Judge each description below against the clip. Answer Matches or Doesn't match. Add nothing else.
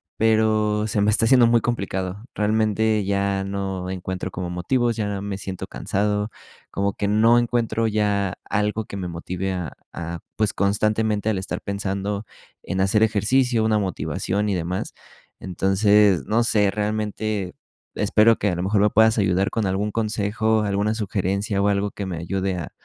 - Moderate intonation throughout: Doesn't match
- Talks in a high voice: Doesn't match